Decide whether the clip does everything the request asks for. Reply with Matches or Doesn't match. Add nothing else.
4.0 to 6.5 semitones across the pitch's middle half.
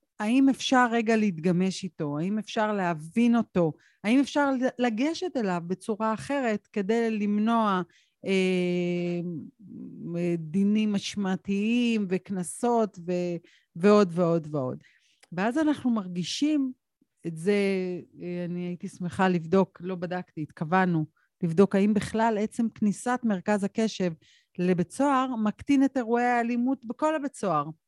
Matches